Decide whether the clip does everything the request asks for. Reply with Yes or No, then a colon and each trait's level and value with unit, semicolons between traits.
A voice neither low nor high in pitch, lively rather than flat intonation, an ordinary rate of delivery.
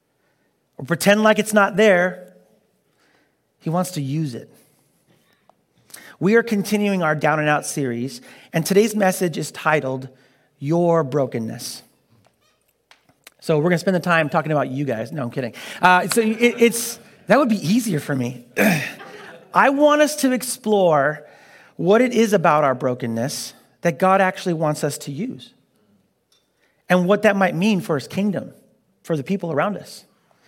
Yes: medium, 180 Hz; wide, 5.9 semitones; average, 155 wpm